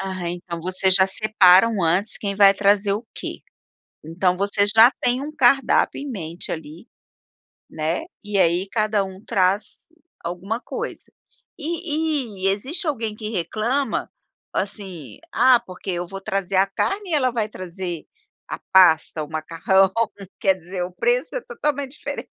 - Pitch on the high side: Yes, high, 195 Hz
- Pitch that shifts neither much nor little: Yes, average, 4.7 semitones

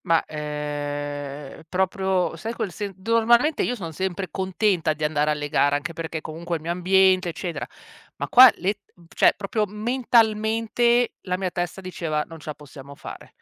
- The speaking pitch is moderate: Yes, medium, 180 Hz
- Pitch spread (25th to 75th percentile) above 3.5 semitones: Yes, wide, 5.6 semitones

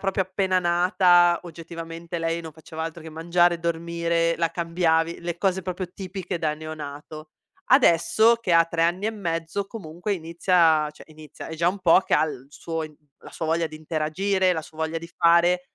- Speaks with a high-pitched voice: No, medium, 170 Hz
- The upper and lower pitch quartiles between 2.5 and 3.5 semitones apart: No, narrow, 1.9 semitones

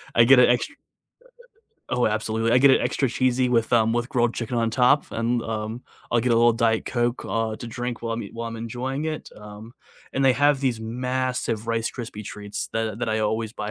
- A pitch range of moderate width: No, narrow, 1.9 semitones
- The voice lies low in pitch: Yes, low, 115 Hz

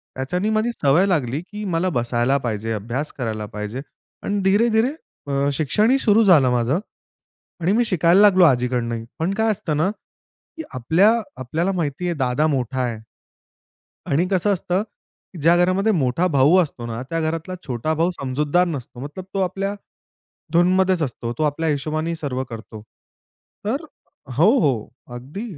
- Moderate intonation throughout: No, wide, 6.4 semitones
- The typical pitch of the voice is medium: Yes, medium, 160 Hz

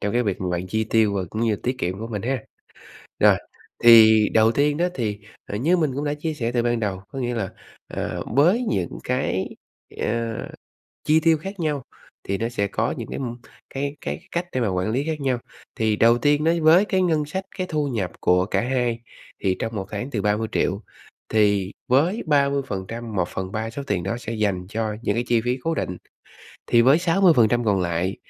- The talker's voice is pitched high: No, low, 115 Hz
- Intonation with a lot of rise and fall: Yes, wide, 5.7 semitones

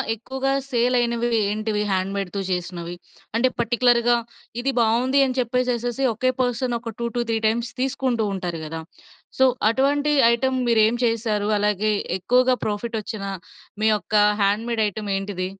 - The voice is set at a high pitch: Yes, high, 230 Hz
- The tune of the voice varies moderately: Yes, average, 3.2 semitones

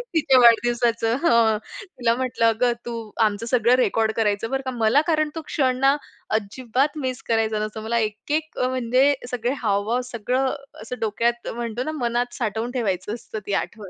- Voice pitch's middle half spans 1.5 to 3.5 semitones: Yes, narrow, 2.4 semitones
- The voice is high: Yes, high, 235 Hz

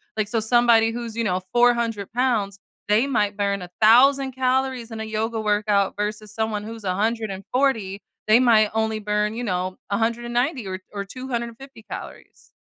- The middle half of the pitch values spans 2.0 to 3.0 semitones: Yes, narrow, 2.5 semitones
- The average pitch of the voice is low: No, high, 220 Hz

